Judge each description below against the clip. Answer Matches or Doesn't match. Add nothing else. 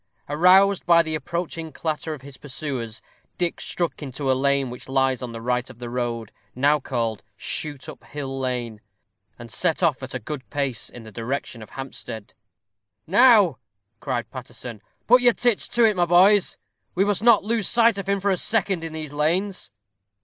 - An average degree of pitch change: Doesn't match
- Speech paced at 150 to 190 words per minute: Matches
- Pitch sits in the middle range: Matches